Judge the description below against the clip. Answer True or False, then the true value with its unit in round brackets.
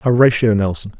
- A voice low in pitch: True (110 Hz)